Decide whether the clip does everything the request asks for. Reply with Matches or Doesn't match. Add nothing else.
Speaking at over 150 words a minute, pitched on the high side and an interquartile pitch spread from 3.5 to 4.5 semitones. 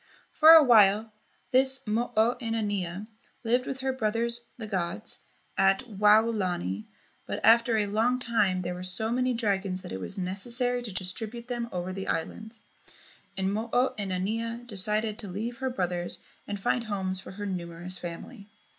Matches